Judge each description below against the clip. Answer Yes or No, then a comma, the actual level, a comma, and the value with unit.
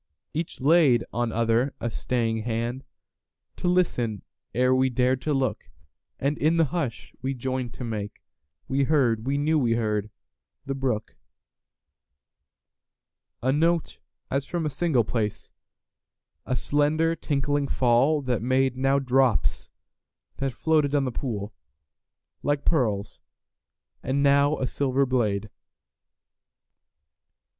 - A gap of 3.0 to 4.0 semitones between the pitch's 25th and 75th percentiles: Yes, average, 3.7 semitones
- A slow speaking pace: Yes, slow, 105 wpm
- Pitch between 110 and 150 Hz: Yes, low, 130 Hz